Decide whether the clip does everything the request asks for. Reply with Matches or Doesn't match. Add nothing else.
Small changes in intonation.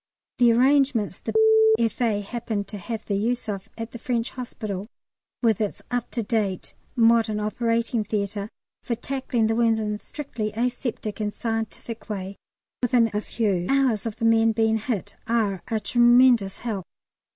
Matches